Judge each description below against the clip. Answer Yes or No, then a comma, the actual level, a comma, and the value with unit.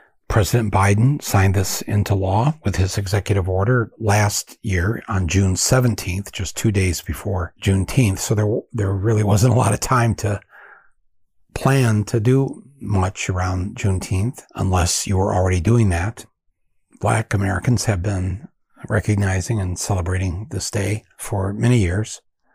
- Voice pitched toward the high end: No, low, 100 Hz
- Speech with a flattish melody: No, average, 3.1 semitones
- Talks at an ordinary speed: Yes, average, 145 wpm